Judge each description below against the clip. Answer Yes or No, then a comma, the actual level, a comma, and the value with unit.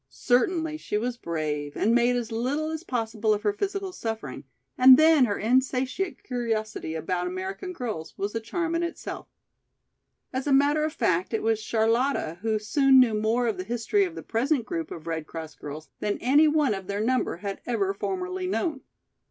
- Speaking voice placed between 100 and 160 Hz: No, high, 235 Hz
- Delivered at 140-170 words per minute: No, average, 185 wpm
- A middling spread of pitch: No, wide, 6.0 semitones